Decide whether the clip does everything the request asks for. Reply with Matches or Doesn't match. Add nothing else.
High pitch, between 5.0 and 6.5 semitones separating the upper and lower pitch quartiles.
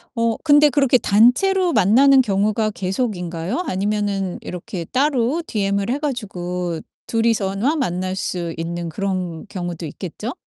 Matches